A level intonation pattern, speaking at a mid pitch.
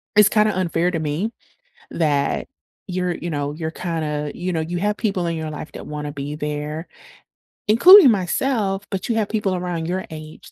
No: average, 4.4 semitones; medium, 175 Hz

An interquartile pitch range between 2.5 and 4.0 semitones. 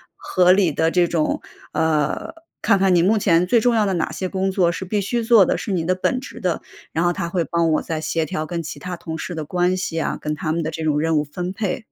Yes: average, 2.8 semitones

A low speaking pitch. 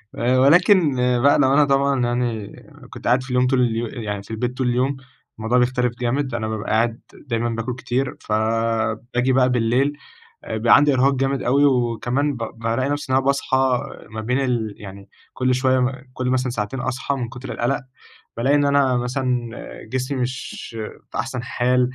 Yes: low, 125 Hz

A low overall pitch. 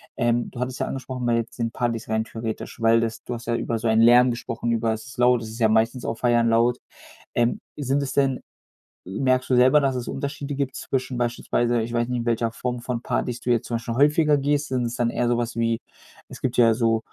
Yes: low, 120 Hz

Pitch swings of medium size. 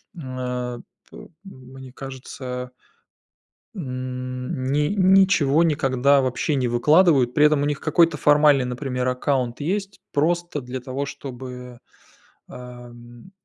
Yes: average, 3.1 semitones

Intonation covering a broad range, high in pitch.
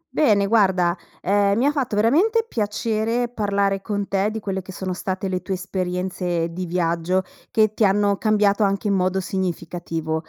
No: narrow, 2.6 semitones; high, 195 Hz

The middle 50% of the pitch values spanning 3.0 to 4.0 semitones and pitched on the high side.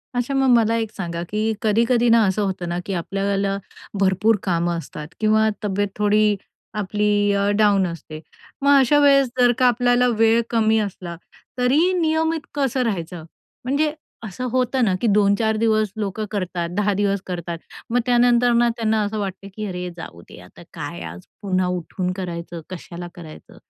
No: average, 4.5 semitones; high, 210 Hz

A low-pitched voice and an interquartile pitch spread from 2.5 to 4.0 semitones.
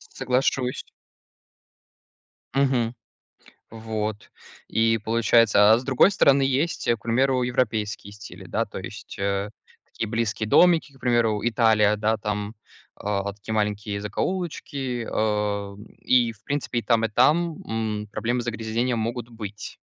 Yes: low, 115 Hz; average, 2.9 semitones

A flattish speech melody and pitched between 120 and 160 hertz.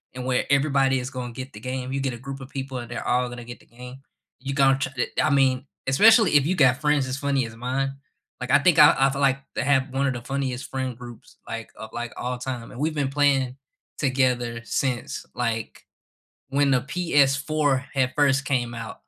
Yes: narrow, 2.0 semitones; low, 135 Hz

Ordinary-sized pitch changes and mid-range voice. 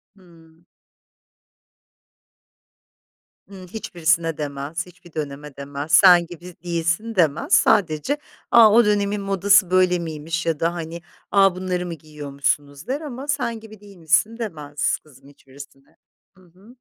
Yes: average, 4.5 semitones; medium, 170 Hz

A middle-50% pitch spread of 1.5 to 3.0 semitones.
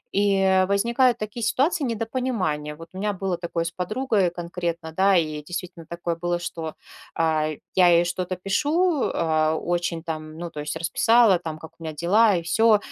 No: average, 4.2 semitones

